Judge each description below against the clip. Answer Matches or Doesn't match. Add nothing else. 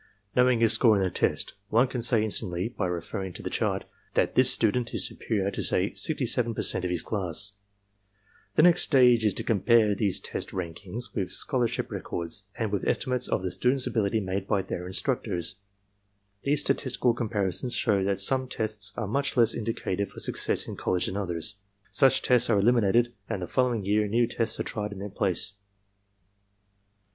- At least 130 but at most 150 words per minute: Doesn't match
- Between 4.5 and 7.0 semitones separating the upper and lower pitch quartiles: Doesn't match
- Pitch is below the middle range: Matches